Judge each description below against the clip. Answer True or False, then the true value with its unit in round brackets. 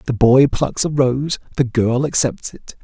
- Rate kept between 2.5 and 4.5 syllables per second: True (4.1 syllables/s)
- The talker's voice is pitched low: True (130 Hz)